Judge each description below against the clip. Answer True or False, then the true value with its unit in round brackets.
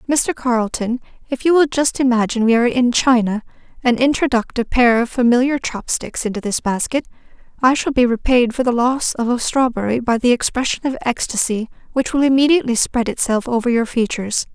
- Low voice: False (245 Hz)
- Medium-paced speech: True (180 wpm)